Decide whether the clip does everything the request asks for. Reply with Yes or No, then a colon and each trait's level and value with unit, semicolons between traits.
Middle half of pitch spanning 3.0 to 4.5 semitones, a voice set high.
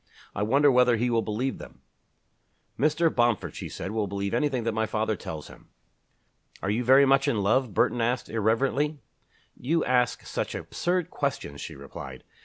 No: average, 4.1 semitones; low, 120 Hz